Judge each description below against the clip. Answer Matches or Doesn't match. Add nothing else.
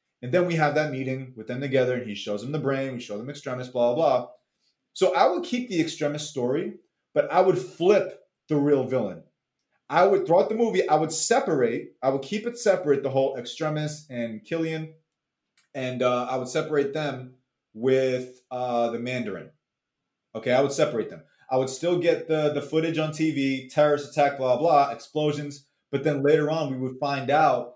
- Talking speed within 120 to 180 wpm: Doesn't match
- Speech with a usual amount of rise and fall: Matches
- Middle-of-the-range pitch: Matches